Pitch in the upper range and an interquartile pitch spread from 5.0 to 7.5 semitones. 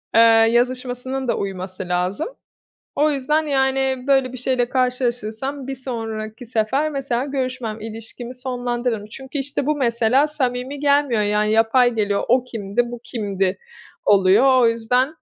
No: high, 245 Hz; average, 3.1 semitones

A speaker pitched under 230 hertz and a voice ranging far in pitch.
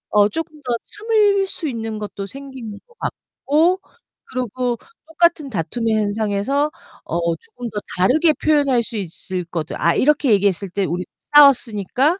No: high, 245 Hz; wide, 6.7 semitones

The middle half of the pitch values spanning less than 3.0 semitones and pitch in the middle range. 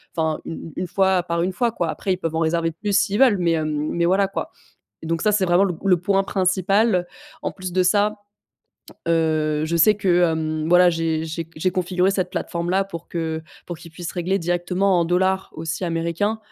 Yes: narrow, 2.6 semitones; medium, 175 Hz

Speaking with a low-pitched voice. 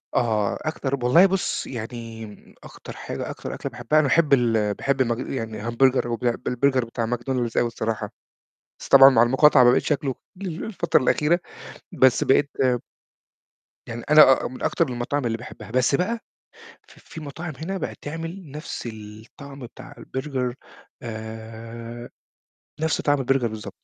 Yes: low, 130 Hz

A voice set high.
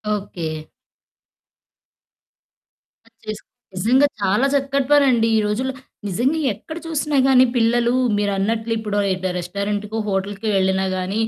Yes: high, 220 Hz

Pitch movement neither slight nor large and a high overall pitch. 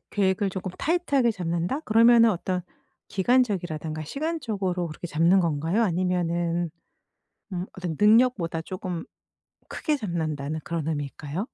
No: average, 4.7 semitones; medium, 180 Hz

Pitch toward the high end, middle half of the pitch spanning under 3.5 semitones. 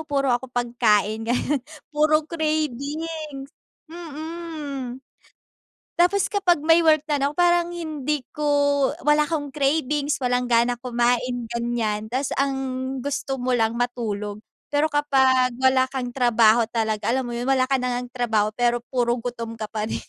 No: very high, 260 Hz; average, 3.8 semitones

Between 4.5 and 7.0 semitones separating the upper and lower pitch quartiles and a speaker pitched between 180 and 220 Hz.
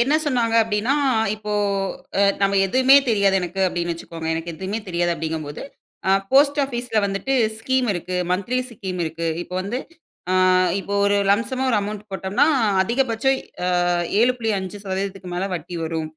Yes: average, 4.9 semitones; high, 200 Hz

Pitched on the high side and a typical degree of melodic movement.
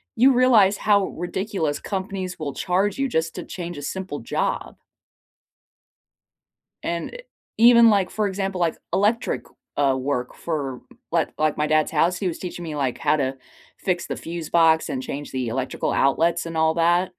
No: medium, 170 Hz; average, 4.4 semitones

